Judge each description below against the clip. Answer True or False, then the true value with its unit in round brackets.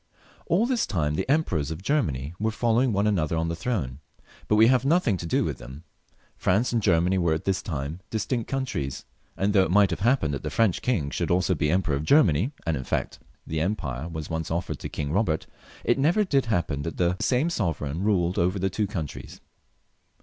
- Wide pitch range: True (6.2 semitones)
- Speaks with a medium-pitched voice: False (90 Hz)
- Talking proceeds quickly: True (220 wpm)